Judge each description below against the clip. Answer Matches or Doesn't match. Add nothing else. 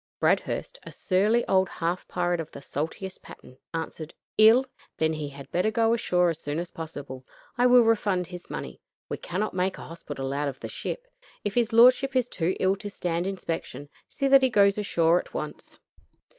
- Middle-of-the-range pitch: Matches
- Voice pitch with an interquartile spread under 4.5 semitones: Doesn't match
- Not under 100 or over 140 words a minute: Doesn't match